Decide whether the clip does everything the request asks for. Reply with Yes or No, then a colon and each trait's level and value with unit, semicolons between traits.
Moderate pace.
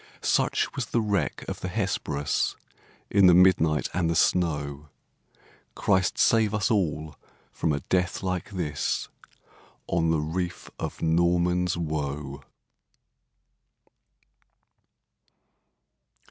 No: slow, 105 wpm